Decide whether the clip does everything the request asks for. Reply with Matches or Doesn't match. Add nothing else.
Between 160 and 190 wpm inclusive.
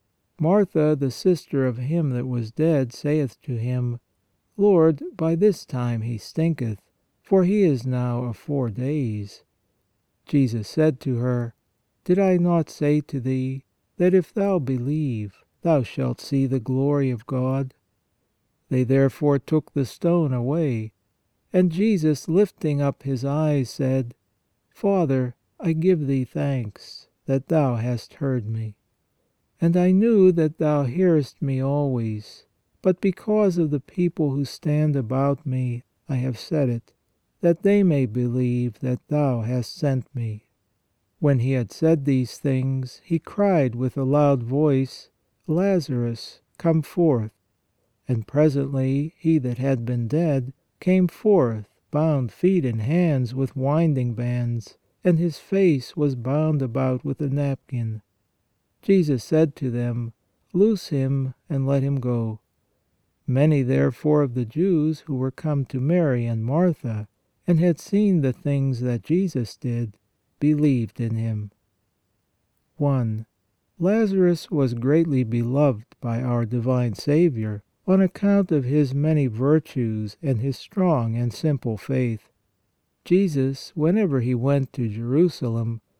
Doesn't match